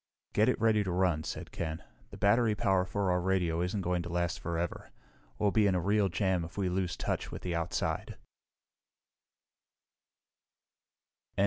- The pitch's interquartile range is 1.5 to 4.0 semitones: Yes, average, 2.7 semitones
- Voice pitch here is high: No, very low, 90 Hz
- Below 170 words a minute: Yes, average, 160 wpm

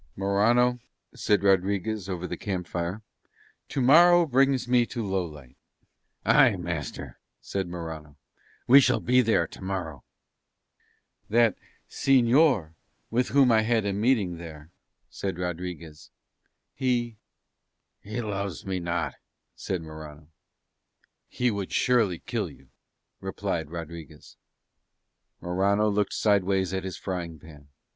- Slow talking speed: Yes, slow, 115 wpm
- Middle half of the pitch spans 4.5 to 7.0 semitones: Yes, average, 5.3 semitones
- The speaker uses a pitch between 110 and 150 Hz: No, very low, 95 Hz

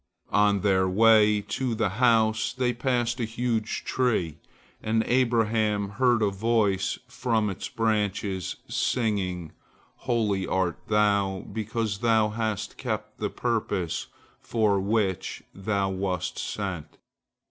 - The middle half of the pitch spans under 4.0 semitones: Yes, average, 2.8 semitones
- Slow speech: Yes, slow, 115 wpm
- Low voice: Yes, low, 105 Hz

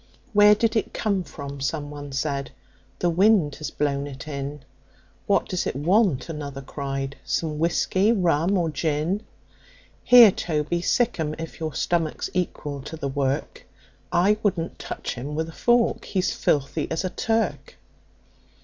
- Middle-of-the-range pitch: Yes, medium, 160 Hz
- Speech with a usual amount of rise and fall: Yes, average, 4.7 semitones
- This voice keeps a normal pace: Yes, average, 155 wpm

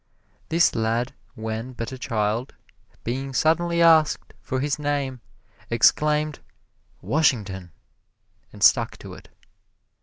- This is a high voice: No, low, 130 Hz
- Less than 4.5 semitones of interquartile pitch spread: No, average, 4.9 semitones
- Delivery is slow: Yes, slow, 110 wpm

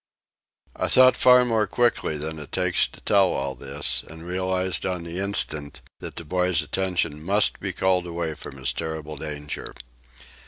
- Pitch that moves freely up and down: No, average, 3.8 semitones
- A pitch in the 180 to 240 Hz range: No, very low, 85 Hz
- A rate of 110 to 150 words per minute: No, average, 165 wpm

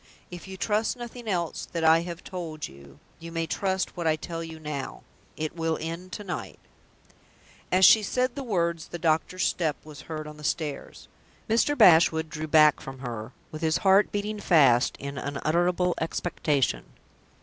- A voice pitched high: No, medium, 165 Hz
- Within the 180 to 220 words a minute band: No, average, 170 wpm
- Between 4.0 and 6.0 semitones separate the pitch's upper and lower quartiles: No, average, 3.1 semitones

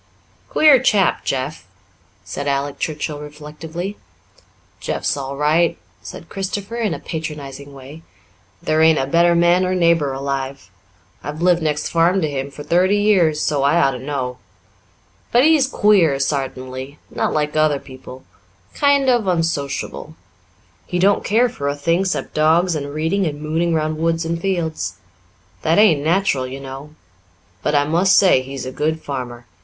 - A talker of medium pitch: Yes, medium, 155 Hz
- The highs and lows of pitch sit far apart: No, average, 4.0 semitones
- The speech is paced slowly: No, average, 160 wpm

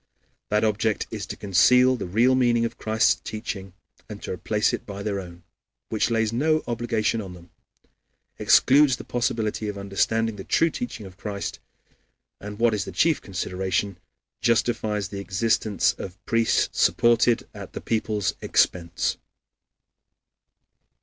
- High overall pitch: No, low, 110 Hz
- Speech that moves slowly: No, average, 145 wpm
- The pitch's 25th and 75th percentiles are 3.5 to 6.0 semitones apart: No, average, 2.9 semitones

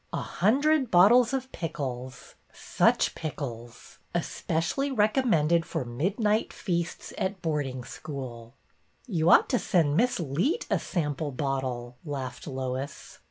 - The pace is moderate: No, slow, 130 wpm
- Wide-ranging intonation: Yes, wide, 8.0 semitones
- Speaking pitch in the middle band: Yes, medium, 160 Hz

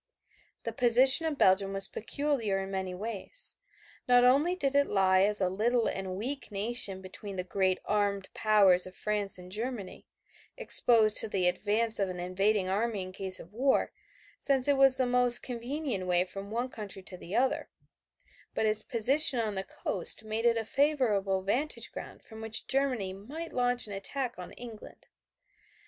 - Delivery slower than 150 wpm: No, average, 175 wpm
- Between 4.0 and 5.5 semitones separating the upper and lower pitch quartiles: Yes, average, 4.4 semitones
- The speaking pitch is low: No, high, 215 Hz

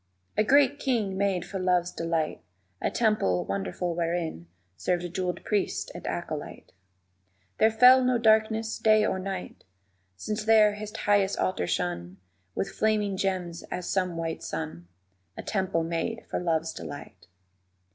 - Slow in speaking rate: No, average, 145 wpm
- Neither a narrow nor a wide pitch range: Yes, average, 4.5 semitones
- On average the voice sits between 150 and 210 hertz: Yes, medium, 185 Hz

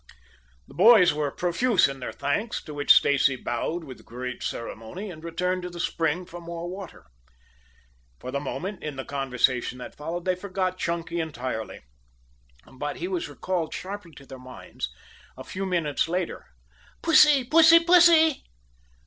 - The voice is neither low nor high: Yes, medium, 170 Hz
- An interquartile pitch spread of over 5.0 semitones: Yes, wide, 5.4 semitones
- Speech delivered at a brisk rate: No, average, 155 wpm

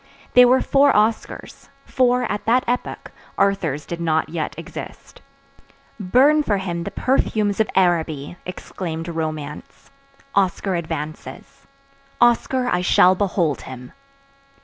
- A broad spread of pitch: Yes, wide, 6.4 semitones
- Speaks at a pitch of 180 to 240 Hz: Yes, medium, 185 Hz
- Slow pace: Yes, slow, 120 wpm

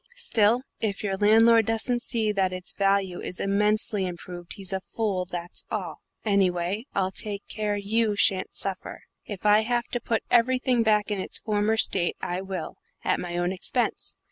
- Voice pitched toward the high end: Yes, high, 205 Hz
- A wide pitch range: No, average, 2.9 semitones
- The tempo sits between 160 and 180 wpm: Yes, average, 170 wpm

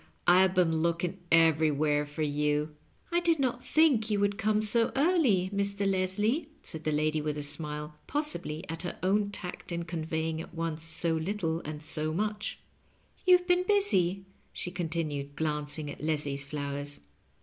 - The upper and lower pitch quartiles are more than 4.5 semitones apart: Yes, average, 5.2 semitones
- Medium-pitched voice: Yes, medium, 165 Hz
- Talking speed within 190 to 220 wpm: No, average, 165 wpm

